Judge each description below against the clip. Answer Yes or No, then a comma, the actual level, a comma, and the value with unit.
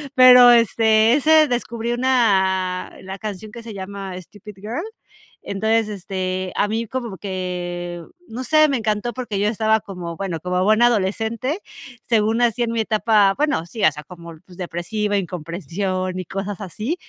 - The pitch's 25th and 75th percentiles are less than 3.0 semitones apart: No, average, 3.8 semitones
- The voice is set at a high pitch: Yes, high, 210 Hz